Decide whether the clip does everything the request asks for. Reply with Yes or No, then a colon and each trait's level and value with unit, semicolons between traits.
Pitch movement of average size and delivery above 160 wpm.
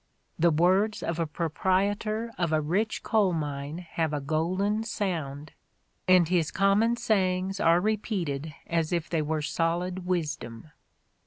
No: average, 4.0 semitones; average, 140 wpm